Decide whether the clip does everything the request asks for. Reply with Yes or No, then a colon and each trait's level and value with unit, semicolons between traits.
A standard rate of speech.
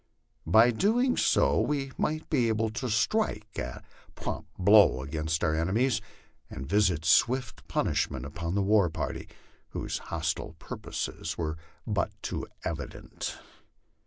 No: slow, 130 wpm